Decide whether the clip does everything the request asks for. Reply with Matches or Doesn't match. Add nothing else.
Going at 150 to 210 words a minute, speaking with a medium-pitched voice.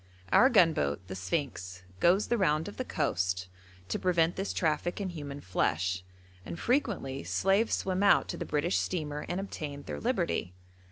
Matches